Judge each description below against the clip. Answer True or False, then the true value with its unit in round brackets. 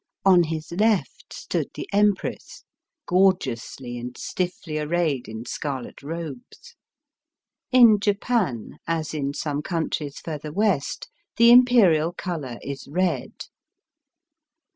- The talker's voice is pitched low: False (165 Hz)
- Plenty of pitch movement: True (5.7 semitones)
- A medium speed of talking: False (105 wpm)